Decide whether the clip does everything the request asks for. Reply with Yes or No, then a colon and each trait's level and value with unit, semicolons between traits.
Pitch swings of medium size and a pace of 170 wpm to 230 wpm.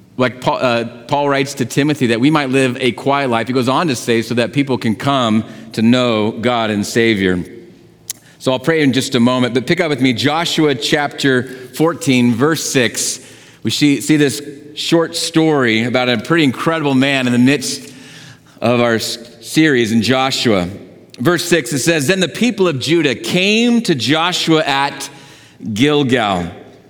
Yes: average, 4.2 semitones; average, 175 wpm